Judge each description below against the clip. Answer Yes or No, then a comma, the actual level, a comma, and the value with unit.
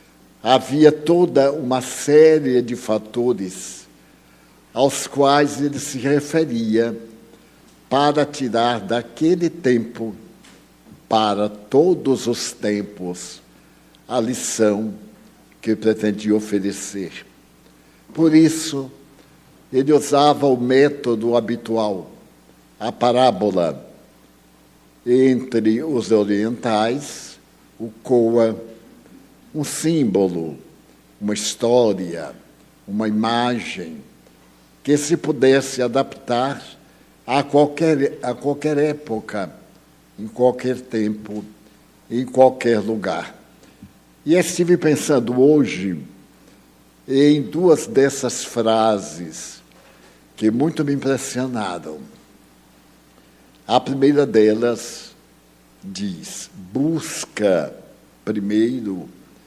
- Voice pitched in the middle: No, low, 120 Hz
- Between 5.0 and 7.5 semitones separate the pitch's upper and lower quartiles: Yes, wide, 5.4 semitones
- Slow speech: Yes, slow, 80 wpm